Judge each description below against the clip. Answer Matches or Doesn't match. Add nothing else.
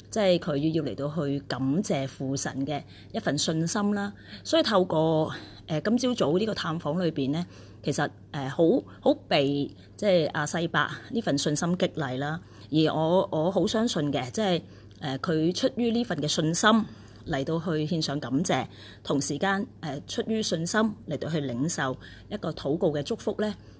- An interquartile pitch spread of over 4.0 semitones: Matches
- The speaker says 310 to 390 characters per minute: Doesn't match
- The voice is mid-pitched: Matches